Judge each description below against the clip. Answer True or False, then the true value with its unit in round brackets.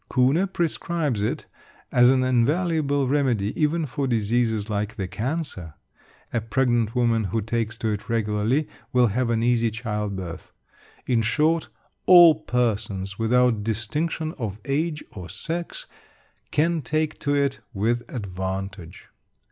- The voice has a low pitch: True (120 Hz)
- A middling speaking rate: False (130 wpm)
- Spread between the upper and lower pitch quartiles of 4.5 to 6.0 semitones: True (5.4 semitones)